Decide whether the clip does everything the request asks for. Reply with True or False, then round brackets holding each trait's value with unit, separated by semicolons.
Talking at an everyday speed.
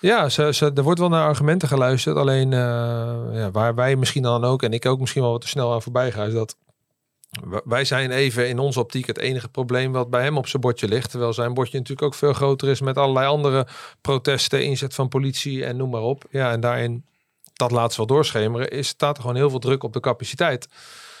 False (235 wpm)